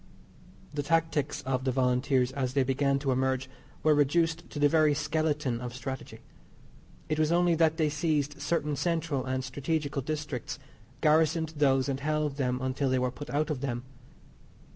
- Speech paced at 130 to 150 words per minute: No, average, 165 wpm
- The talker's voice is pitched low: No, medium, 145 Hz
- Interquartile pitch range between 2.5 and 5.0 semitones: Yes, average, 2.9 semitones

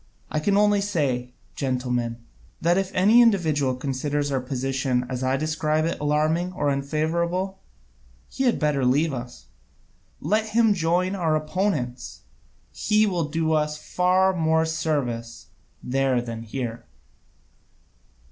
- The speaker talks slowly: Yes, slow, 130 wpm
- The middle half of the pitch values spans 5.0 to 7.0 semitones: Yes, wide, 5.6 semitones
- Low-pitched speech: No, medium, 155 Hz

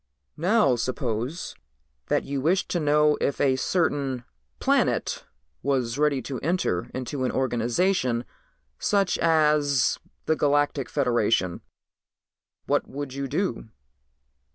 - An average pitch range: Yes, average, 3.2 semitones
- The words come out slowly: Yes, slow, 110 wpm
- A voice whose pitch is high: No, medium, 140 Hz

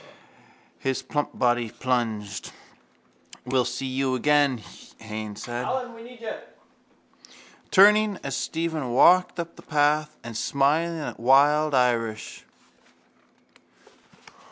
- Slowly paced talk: Yes, slow, 90 wpm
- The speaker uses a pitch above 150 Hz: No, low, 135 Hz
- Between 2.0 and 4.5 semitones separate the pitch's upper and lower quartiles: Yes, average, 4.0 semitones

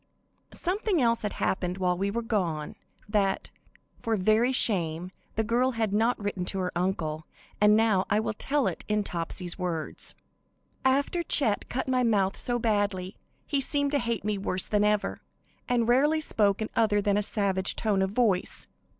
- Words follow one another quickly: No, average, 175 wpm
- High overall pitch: Yes, high, 210 Hz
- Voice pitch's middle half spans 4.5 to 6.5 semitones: No, average, 3.8 semitones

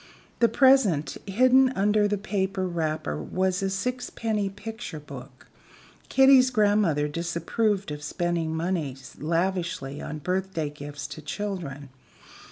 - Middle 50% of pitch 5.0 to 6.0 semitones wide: Yes, wide, 5.5 semitones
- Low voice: No, medium, 185 Hz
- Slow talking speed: Yes, slow, 115 wpm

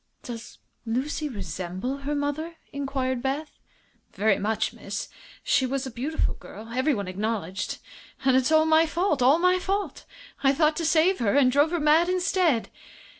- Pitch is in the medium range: No, very high, 275 Hz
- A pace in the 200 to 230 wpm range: No, average, 160 wpm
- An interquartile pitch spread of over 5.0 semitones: Yes, wide, 5.4 semitones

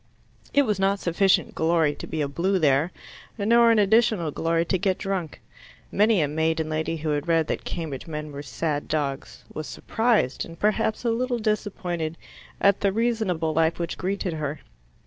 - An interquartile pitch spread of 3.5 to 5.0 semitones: Yes, average, 4.7 semitones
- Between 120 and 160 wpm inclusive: No, average, 175 wpm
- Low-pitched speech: No, medium, 170 Hz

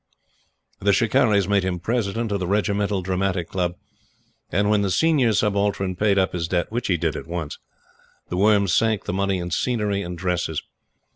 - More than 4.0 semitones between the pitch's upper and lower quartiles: No, average, 2.7 semitones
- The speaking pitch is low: Yes, low, 100 Hz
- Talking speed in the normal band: Yes, average, 175 wpm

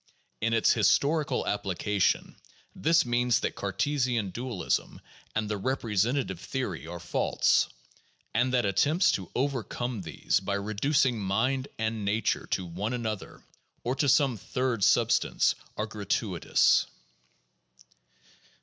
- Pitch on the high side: No, low, 110 Hz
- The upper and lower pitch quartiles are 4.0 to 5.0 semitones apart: Yes, average, 4.3 semitones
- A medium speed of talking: No, slow, 120 wpm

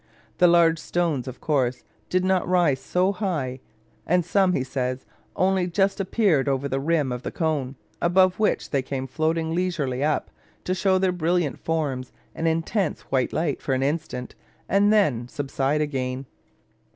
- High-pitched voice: No, medium, 160 Hz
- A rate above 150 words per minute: Yes, average, 165 wpm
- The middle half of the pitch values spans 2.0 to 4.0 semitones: No, average, 5.2 semitones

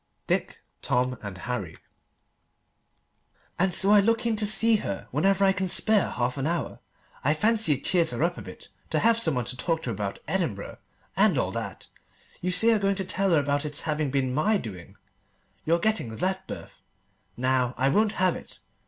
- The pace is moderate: Yes, average, 195 wpm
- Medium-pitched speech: Yes, medium, 165 Hz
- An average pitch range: No, wide, 7.5 semitones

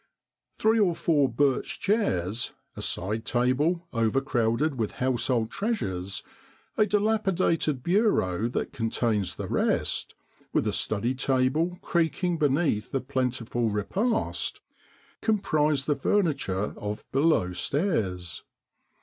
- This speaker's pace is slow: Yes, slow, 105 wpm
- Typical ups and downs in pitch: No, wide, 7.4 semitones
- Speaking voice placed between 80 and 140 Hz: Yes, low, 135 Hz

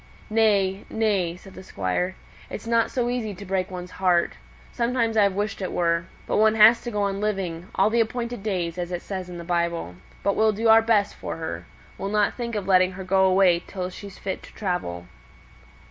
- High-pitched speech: Yes, high, 195 Hz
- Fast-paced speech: Yes, fast, 210 wpm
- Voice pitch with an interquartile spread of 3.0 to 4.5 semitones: Yes, average, 3.3 semitones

